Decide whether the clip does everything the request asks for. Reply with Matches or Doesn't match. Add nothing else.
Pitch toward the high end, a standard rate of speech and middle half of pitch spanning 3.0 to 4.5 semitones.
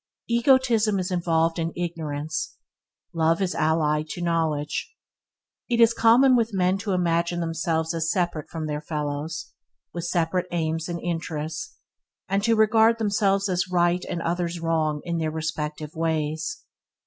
Doesn't match